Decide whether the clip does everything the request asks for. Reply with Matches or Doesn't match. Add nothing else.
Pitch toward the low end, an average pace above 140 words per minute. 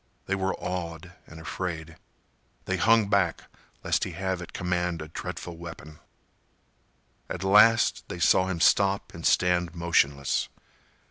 Doesn't match